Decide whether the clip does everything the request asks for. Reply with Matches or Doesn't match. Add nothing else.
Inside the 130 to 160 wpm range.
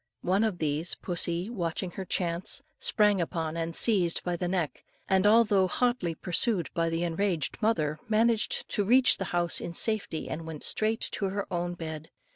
Doesn't match